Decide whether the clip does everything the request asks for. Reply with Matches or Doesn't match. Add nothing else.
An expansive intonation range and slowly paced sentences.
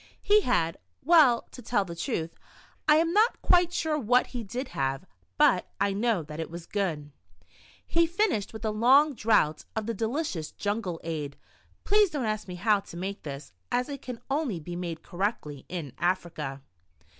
Doesn't match